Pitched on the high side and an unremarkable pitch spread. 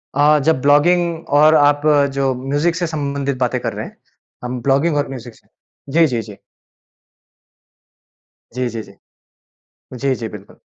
No: medium, 140 Hz; average, 3.3 semitones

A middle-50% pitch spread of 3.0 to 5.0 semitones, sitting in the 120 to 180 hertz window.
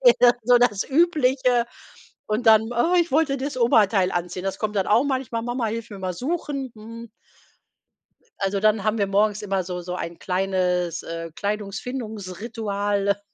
No: average, 4.1 semitones; high, 215 Hz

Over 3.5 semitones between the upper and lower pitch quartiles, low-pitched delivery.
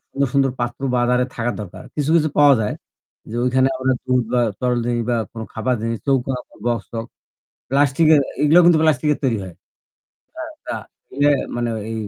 No: average, 2.8 semitones; low, 125 Hz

